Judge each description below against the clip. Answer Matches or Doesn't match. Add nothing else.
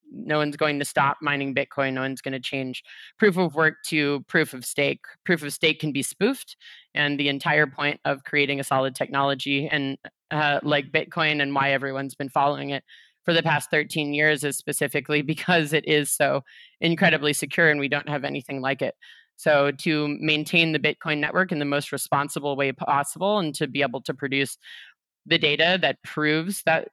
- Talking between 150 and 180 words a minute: Doesn't match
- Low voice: Doesn't match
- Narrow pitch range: Matches